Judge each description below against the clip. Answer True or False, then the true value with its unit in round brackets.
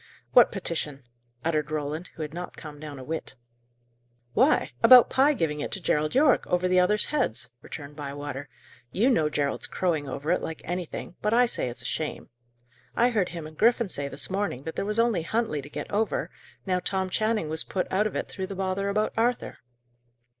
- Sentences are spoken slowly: False (200 wpm)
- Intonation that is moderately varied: False (6.0 semitones)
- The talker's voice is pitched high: False (180 Hz)